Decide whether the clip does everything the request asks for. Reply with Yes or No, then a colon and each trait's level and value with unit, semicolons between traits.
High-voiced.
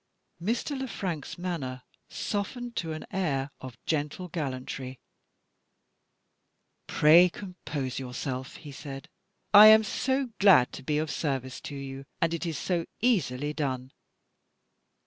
No: medium, 155 Hz